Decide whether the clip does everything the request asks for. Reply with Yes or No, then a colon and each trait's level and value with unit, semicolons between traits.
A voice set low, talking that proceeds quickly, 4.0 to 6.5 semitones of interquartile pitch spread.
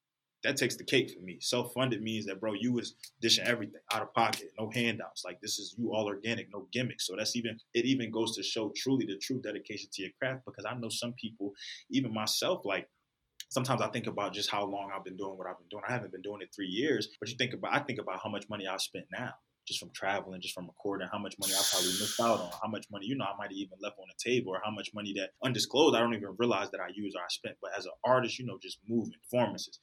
No: low, 105 Hz; fast, 275 wpm; average, 3.1 semitones